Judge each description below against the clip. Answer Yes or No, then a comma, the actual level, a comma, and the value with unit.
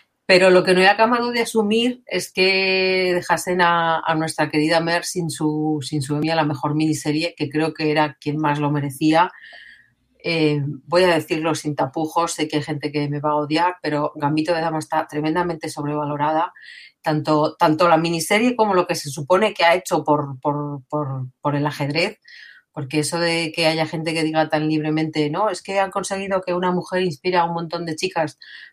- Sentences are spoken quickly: Yes, fast, 200 wpm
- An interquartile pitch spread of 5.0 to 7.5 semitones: No, average, 2.7 semitones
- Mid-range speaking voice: Yes, medium, 160 Hz